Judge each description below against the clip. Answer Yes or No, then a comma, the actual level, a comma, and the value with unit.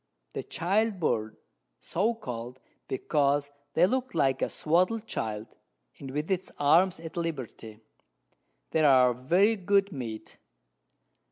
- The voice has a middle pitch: Yes, medium, 155 Hz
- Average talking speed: No, slow, 115 wpm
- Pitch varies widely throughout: Yes, wide, 6.7 semitones